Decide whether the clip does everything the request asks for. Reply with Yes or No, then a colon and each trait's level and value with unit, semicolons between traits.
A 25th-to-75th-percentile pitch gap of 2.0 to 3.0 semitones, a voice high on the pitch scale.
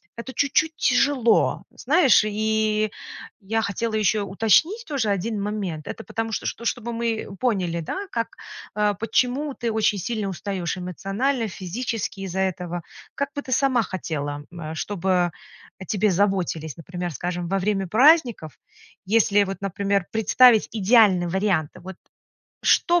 No: average, 4.1 semitones; high, 210 Hz